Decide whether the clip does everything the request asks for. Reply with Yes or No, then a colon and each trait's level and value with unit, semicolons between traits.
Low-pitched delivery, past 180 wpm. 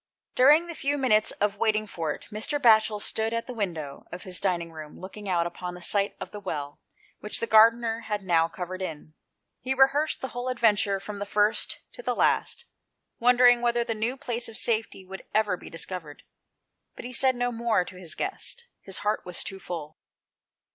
No: high, 210 Hz; average, 195 wpm